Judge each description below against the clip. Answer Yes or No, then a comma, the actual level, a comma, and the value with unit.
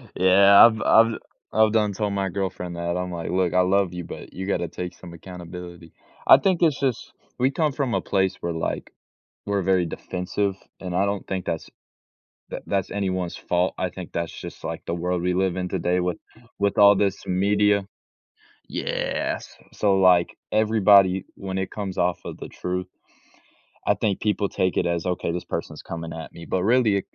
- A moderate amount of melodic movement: No, narrow, 2.2 semitones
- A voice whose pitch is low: Yes, very low, 95 Hz